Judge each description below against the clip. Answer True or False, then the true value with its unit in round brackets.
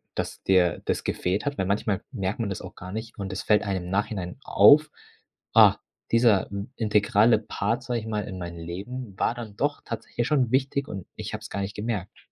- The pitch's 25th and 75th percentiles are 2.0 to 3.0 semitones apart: False (3.5 semitones)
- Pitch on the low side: True (105 Hz)